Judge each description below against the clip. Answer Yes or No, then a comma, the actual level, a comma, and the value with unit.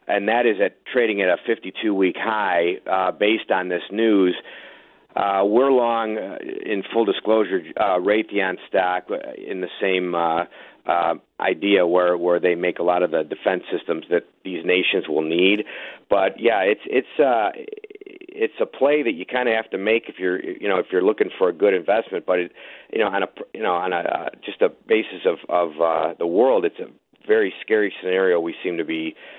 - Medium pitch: No, low, 110 Hz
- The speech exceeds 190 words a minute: Yes, average, 200 wpm